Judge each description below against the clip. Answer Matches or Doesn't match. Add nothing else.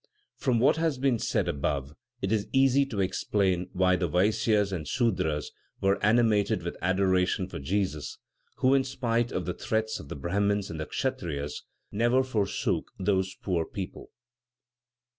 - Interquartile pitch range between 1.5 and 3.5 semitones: Doesn't match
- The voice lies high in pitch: Doesn't match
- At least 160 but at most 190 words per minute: Doesn't match